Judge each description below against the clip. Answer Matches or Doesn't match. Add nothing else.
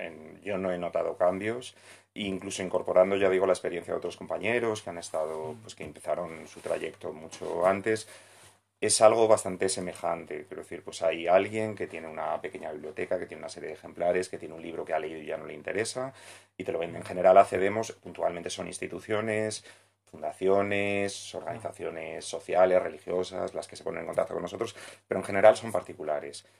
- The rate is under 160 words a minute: Doesn't match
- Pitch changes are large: Doesn't match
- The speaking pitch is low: Matches